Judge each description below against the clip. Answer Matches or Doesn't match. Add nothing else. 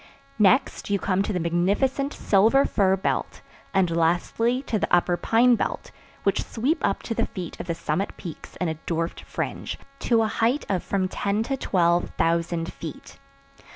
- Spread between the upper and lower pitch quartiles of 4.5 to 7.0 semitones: Matches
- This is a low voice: Doesn't match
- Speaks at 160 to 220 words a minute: Matches